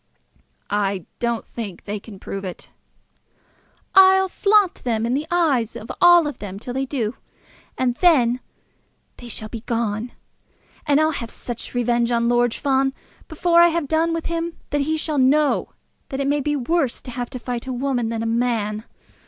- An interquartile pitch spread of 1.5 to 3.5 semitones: No, average, 4.9 semitones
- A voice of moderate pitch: No, very high, 250 Hz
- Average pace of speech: Yes, average, 180 wpm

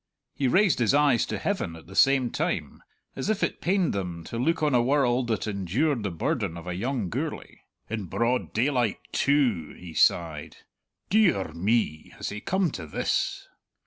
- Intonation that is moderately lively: No, wide, 7.9 semitones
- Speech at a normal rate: Yes, average, 180 wpm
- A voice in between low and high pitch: No, low, 120 Hz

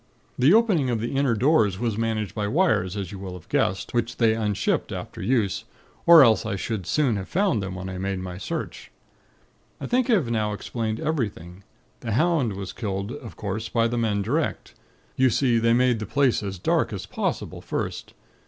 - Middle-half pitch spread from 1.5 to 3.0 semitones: No, average, 4.5 semitones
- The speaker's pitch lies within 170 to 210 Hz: No, low, 115 Hz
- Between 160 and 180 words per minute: No, average, 200 wpm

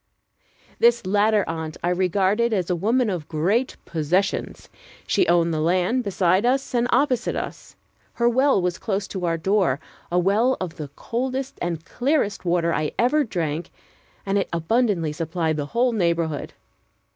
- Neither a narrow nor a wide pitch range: No, wide, 5.8 semitones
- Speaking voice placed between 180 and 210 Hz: Yes, high, 190 Hz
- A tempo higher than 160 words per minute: No, average, 155 wpm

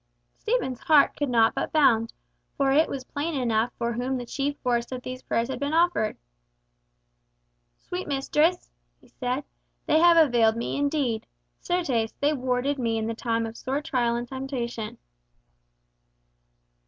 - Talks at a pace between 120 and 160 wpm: Yes, average, 155 wpm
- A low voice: No, very high, 255 Hz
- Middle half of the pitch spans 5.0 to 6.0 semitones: No, average, 3.6 semitones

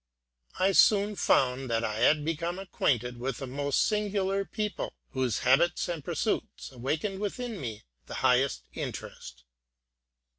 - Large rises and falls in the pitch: Yes, wide, 7.6 semitones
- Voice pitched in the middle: Yes, medium, 150 Hz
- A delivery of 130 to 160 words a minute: Yes, slow, 135 wpm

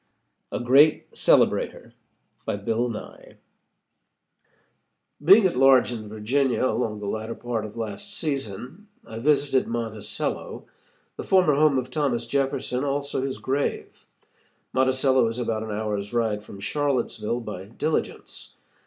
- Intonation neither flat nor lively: Yes, average, 4.1 semitones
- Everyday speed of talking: No, slow, 130 wpm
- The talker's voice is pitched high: No, low, 125 Hz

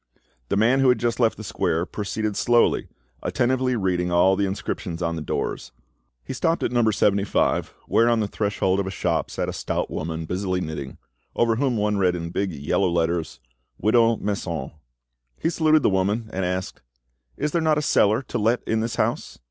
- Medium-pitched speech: No, low, 100 Hz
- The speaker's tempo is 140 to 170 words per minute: No, average, 190 wpm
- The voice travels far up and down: No, average, 4.7 semitones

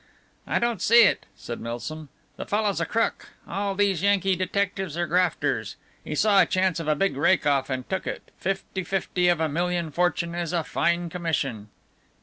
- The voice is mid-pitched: Yes, medium, 175 Hz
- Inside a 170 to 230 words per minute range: Yes, average, 180 wpm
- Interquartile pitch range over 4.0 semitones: No, average, 3.4 semitones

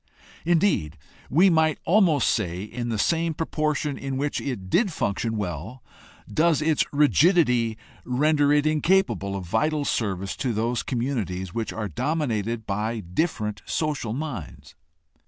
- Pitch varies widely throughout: Yes, wide, 6.5 semitones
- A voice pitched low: Yes, low, 125 Hz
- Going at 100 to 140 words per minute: Yes, slow, 135 wpm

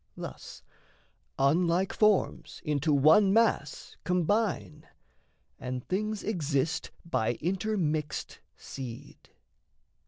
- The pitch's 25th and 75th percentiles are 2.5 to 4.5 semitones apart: No, wide, 5.5 semitones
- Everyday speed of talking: No, slow, 75 wpm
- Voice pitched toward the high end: No, medium, 165 Hz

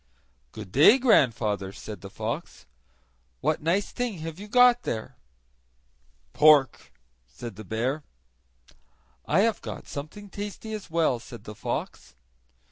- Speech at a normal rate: No, slow, 125 wpm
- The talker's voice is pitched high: No, medium, 150 Hz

